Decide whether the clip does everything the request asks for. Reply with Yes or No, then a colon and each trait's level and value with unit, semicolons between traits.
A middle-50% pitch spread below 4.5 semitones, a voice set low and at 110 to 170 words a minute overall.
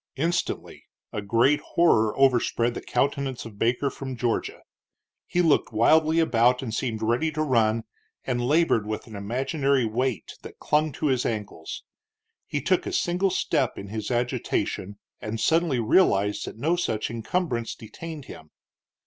No: wide, 5.5 semitones; low, 125 Hz; average, 150 wpm